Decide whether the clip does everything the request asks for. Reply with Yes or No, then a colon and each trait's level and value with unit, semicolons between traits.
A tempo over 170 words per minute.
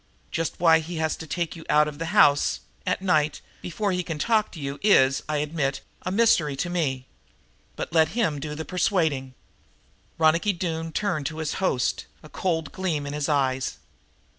Yes: average, 185 wpm